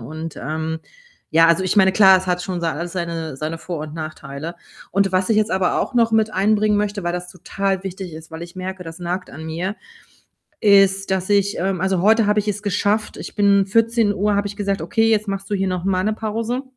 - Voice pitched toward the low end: No, high, 190 Hz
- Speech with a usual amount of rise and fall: Yes, average, 3.1 semitones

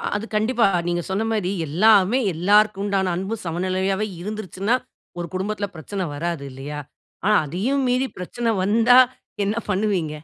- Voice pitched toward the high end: Yes, high, 195 Hz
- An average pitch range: Yes, average, 3.4 semitones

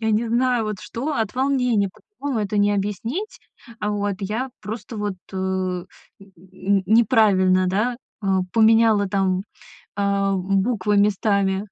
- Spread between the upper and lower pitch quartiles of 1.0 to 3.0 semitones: Yes, average, 2.7 semitones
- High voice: Yes, high, 205 Hz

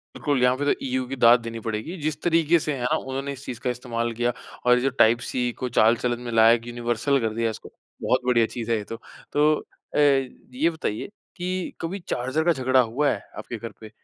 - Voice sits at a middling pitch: No, low, 125 Hz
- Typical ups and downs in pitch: Yes, average, 3.6 semitones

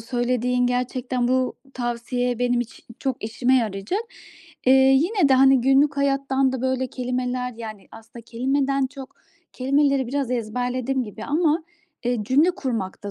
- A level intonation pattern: Yes, narrow, 1.9 semitones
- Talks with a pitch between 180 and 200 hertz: No, very high, 255 Hz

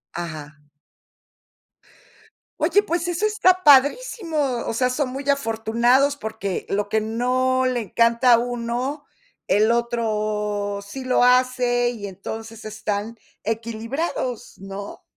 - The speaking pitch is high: Yes, high, 235 Hz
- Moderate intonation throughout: Yes, average, 3.3 semitones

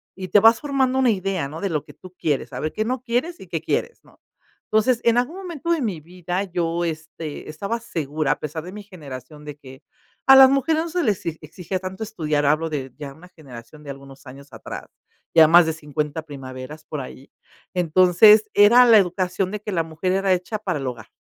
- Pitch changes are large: Yes, wide, 6.0 semitones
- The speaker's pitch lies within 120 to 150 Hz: No, medium, 175 Hz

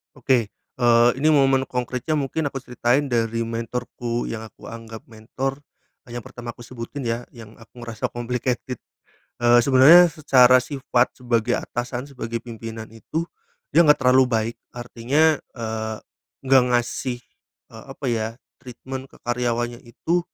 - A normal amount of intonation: No, narrow, 2.2 semitones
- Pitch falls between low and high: No, low, 120 Hz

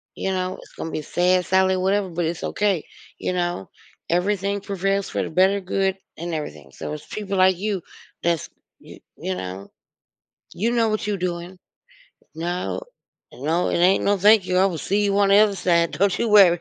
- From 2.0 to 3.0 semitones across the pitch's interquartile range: Yes, narrow, 2.6 semitones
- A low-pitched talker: No, medium, 185 Hz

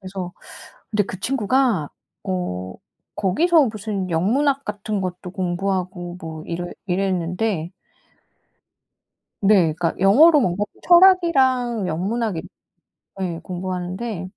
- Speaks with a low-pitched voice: No, high, 190 Hz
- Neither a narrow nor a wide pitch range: Yes, average, 4.6 semitones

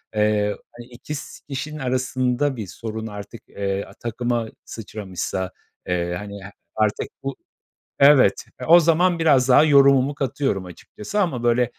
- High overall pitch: No, low, 120 Hz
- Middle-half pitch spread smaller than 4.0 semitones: No, average, 5.1 semitones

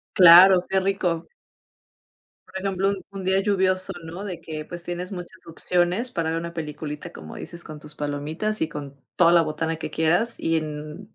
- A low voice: No, medium, 170 Hz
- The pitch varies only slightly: No, average, 3.2 semitones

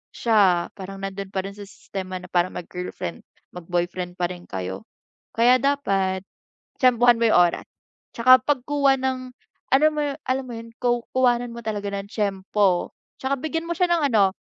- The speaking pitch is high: Yes, high, 210 Hz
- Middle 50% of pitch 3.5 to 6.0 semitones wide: Yes, wide, 5.4 semitones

